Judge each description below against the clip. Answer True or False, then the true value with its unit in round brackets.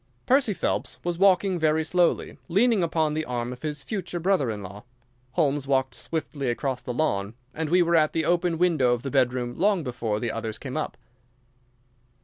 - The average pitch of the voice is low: False (155 Hz)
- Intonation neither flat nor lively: False (5.8 semitones)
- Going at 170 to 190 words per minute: True (185 wpm)